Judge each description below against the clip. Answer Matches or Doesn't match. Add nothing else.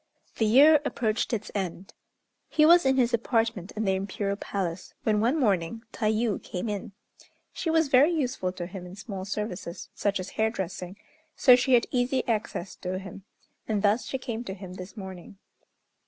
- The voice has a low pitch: Doesn't match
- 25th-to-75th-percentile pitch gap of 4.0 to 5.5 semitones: Matches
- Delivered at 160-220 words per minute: Matches